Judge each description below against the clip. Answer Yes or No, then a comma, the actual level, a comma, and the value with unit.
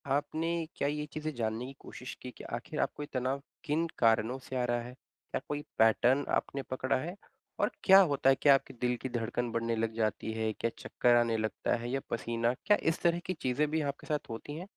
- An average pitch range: Yes, average, 4.1 semitones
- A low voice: Yes, low, 130 Hz